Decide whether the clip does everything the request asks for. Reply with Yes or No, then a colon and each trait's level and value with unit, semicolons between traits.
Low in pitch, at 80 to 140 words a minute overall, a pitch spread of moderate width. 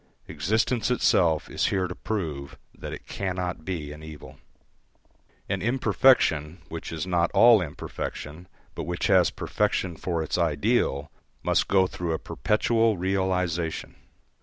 Yes: very low, 90 Hz; slow, 135 wpm; average, 3.5 semitones